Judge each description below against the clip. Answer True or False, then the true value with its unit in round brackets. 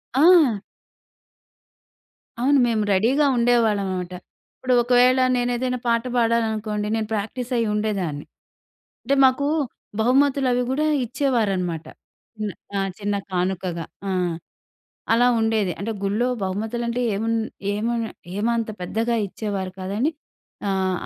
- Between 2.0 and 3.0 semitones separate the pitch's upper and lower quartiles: False (3.6 semitones)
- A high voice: True (225 Hz)